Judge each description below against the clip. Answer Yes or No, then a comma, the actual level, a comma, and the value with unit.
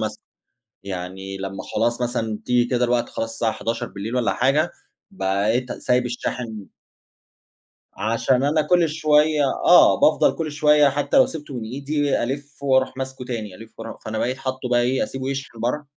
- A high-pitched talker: No, low, 125 Hz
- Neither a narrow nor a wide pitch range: Yes, average, 3.8 semitones